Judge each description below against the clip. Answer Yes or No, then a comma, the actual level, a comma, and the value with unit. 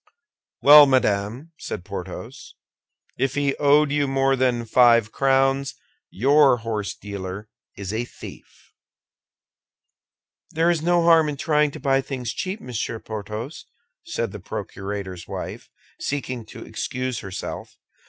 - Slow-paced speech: Yes, slow, 125 wpm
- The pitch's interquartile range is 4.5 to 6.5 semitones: Yes, average, 5.1 semitones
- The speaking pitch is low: Yes, low, 130 Hz